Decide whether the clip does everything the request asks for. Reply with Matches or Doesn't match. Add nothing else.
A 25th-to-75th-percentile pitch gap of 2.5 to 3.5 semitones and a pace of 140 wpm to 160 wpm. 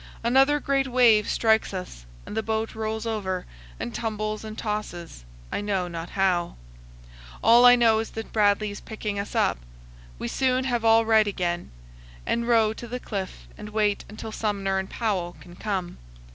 Doesn't match